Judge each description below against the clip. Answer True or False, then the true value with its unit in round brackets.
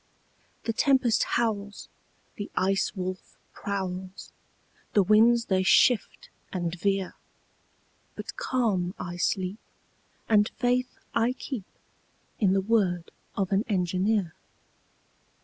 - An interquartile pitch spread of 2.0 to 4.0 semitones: True (3.5 semitones)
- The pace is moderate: False (105 wpm)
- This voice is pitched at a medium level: False (200 Hz)